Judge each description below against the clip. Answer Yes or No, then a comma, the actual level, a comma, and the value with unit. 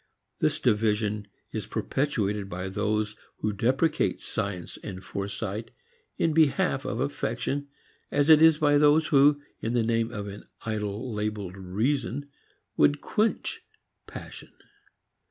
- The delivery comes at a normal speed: No, slow, 125 wpm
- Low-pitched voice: Yes, low, 110 Hz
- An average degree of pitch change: No, wide, 5.9 semitones